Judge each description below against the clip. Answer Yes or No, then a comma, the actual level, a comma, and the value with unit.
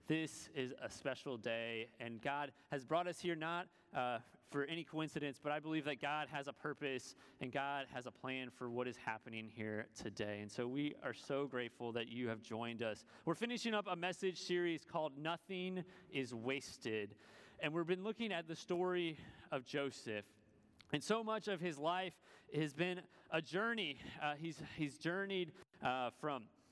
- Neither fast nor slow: Yes, average, 180 wpm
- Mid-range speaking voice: Yes, medium, 145 Hz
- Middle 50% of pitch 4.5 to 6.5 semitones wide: Yes, wide, 5.6 semitones